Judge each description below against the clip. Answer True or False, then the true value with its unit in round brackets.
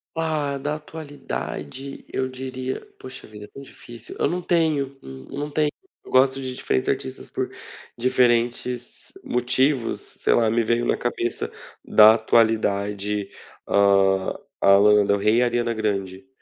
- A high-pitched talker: False (120 Hz)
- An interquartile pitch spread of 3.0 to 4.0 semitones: False (4.4 semitones)